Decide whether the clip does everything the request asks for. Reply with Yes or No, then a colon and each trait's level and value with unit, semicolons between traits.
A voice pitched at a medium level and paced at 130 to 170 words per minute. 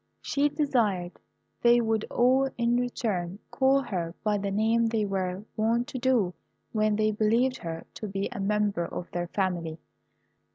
No: high, 215 Hz; average, 160 wpm